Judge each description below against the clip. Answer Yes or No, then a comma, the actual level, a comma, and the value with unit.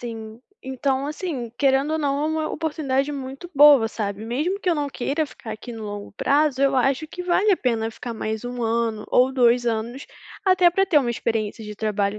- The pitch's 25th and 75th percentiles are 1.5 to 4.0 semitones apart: No, average, 4.8 semitones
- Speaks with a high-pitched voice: Yes, very high, 260 Hz